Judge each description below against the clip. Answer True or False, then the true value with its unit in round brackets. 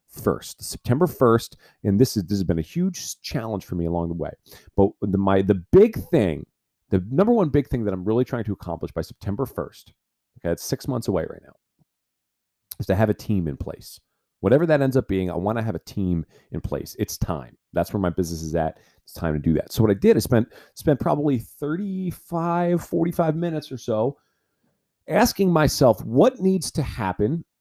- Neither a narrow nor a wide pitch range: False (8.7 semitones)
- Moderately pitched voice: False (110 Hz)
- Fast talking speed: True (210 wpm)